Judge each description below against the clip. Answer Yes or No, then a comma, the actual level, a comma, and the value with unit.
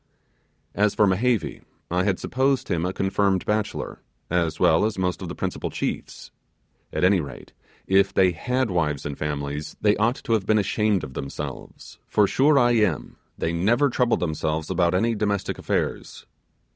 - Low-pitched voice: Yes, very low, 95 Hz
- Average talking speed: Yes, average, 170 wpm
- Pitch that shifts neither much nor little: Yes, average, 4.3 semitones